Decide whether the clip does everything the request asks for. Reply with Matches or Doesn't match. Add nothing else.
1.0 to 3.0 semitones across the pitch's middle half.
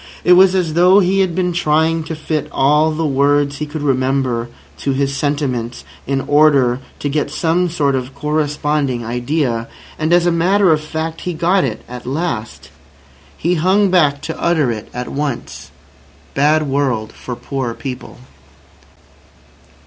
Doesn't match